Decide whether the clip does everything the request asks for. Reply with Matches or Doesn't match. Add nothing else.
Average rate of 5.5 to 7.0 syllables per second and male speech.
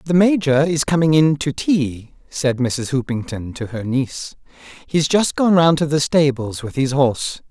Doesn't match